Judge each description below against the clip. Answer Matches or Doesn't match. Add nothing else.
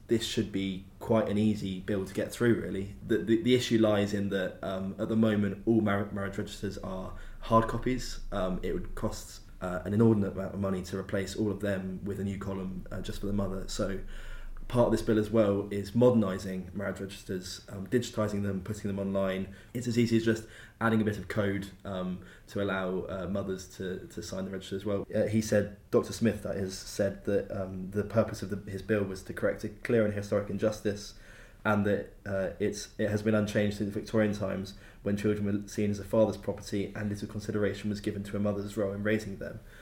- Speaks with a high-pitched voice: Doesn't match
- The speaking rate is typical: Doesn't match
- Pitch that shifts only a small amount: Matches